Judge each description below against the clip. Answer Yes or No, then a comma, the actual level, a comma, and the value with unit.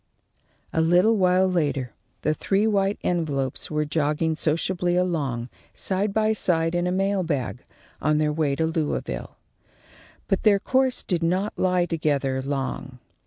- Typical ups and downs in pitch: Yes, average, 4.1 semitones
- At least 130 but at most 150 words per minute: Yes, average, 145 wpm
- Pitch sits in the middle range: Yes, medium, 165 Hz